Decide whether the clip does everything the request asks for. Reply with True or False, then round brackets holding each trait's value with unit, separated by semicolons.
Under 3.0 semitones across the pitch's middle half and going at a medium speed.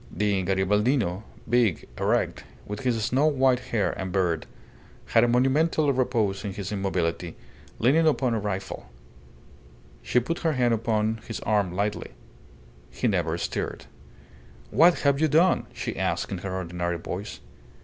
False (5.2 semitones; 145 wpm)